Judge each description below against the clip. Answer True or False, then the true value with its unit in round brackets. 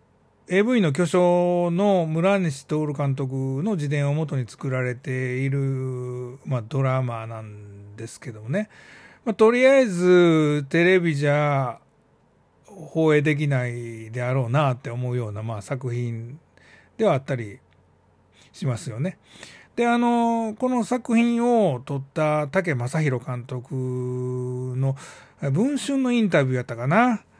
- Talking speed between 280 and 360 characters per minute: False (250 characters per minute)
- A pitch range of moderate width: False (6.1 semitones)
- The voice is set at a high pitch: False (140 Hz)